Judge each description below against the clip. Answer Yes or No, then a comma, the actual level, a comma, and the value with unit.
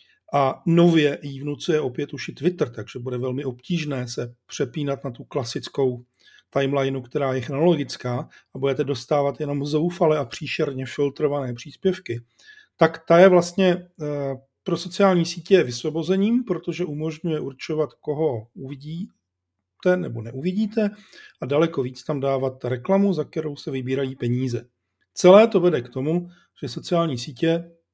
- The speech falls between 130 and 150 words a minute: Yes, average, 135 wpm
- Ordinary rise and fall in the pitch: Yes, average, 4.5 semitones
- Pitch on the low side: No, medium, 150 Hz